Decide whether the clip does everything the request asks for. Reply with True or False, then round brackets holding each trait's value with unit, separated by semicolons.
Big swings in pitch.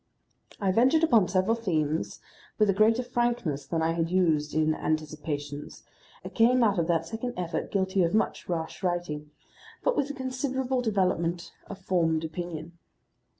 True (5.9 semitones)